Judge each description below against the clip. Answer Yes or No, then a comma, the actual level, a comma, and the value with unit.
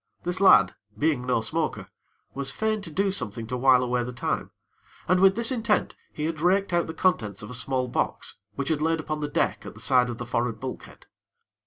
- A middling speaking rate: No, fast, 215 wpm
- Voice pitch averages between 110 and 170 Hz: Yes, medium, 140 Hz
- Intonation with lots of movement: Yes, wide, 6.3 semitones